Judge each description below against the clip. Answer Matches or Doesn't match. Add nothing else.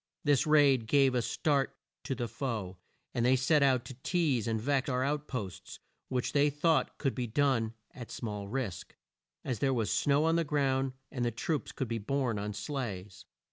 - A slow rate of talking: Doesn't match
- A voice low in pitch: Matches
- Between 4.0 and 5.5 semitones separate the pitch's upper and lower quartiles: Doesn't match